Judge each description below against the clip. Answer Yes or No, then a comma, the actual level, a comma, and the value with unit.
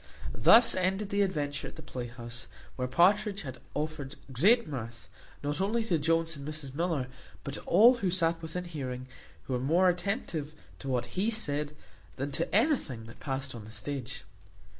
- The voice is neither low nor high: Yes, medium, 155 Hz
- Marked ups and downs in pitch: Yes, wide, 6.0 semitones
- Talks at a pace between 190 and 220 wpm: No, average, 175 wpm